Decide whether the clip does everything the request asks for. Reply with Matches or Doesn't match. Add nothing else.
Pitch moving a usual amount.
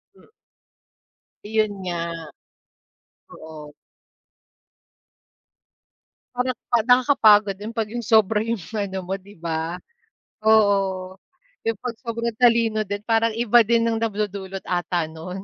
Matches